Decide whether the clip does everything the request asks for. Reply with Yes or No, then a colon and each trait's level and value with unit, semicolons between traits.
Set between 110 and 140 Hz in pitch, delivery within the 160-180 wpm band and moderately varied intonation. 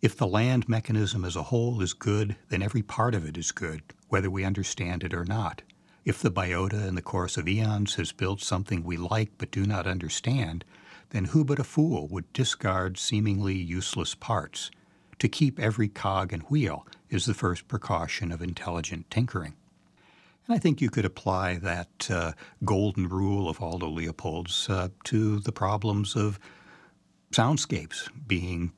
No: very low, 95 Hz; average, 170 wpm; average, 3.6 semitones